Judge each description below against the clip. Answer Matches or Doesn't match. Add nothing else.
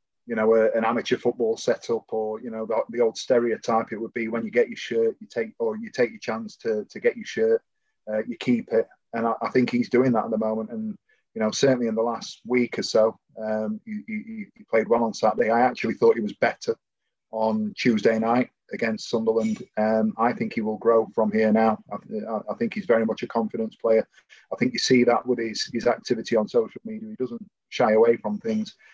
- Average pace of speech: Doesn't match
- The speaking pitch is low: Matches